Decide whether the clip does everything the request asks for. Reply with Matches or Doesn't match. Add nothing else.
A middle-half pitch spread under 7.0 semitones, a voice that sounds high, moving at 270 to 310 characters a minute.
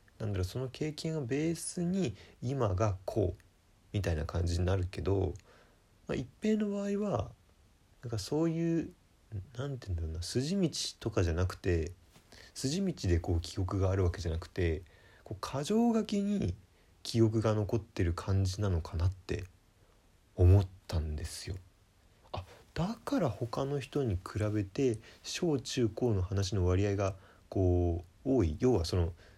Doesn't match